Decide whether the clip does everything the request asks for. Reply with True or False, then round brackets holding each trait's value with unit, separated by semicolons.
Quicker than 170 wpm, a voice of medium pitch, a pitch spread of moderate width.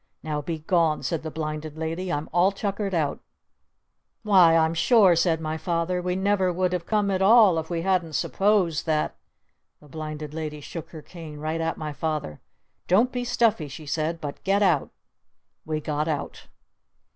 True (180 wpm; 165 Hz; 3.3 semitones)